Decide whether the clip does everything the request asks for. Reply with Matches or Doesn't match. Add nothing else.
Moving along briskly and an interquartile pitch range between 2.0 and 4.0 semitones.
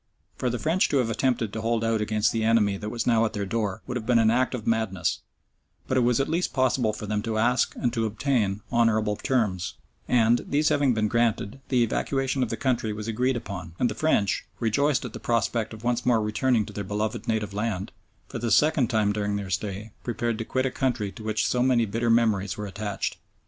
Matches